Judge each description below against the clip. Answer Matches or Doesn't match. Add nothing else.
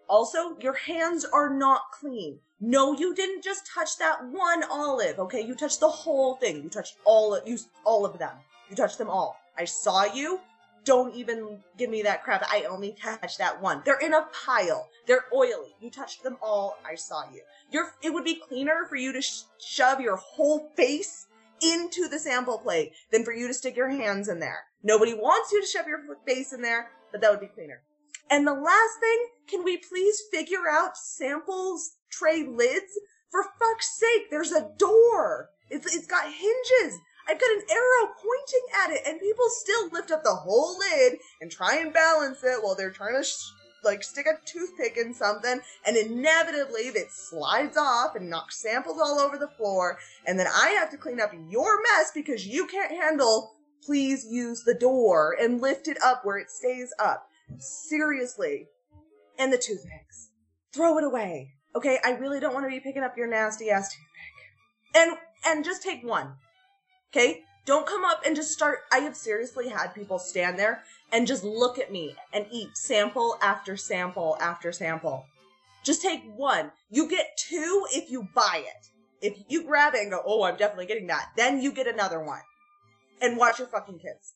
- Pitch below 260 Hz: Doesn't match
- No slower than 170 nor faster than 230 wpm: Matches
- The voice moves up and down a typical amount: Doesn't match